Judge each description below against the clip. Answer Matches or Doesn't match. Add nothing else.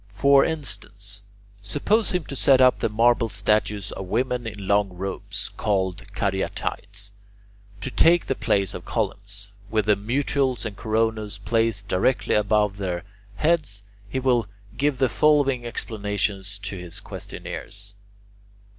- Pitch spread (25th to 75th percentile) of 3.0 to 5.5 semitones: Matches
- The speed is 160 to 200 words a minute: Doesn't match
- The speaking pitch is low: Matches